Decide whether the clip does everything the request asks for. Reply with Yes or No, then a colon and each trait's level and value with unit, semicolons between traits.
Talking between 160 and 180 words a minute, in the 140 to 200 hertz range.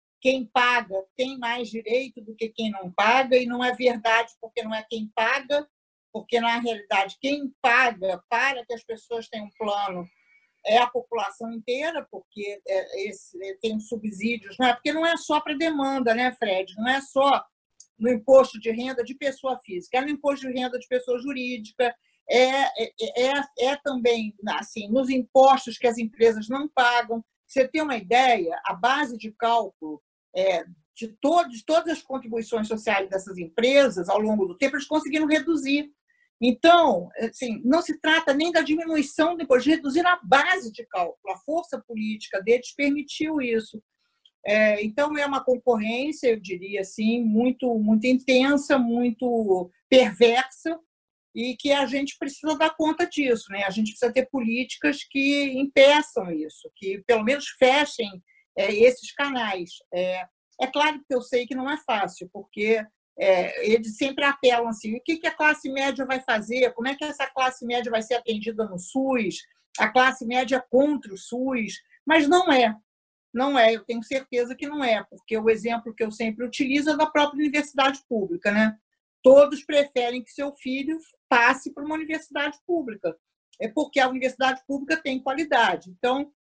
No: average, 170 wpm; very high, 250 Hz